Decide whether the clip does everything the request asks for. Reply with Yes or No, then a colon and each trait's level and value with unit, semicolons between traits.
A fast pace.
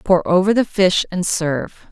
No: average, 190 wpm